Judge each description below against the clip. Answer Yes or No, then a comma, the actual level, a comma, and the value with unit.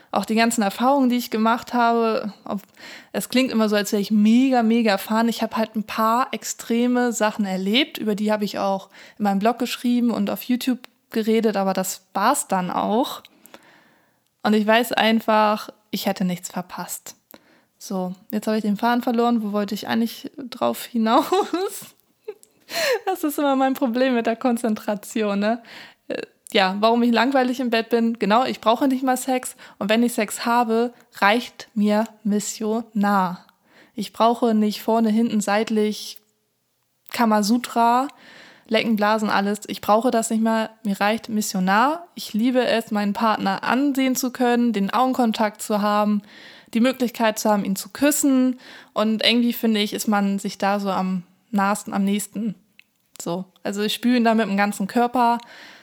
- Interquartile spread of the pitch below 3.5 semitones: Yes, average, 2.8 semitones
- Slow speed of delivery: No, average, 165 wpm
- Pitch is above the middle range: Yes, high, 225 Hz